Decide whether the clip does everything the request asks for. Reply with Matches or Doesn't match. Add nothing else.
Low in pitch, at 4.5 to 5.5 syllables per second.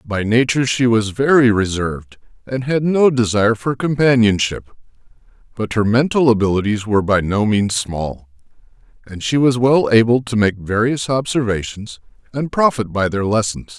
Matches